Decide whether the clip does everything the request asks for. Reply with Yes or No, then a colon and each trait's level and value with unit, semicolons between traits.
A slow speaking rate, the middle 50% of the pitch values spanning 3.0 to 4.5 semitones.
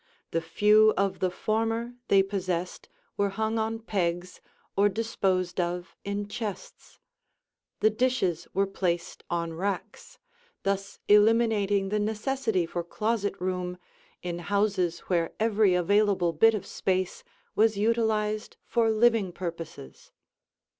Yes: slow, 120 wpm; average, 3.3 semitones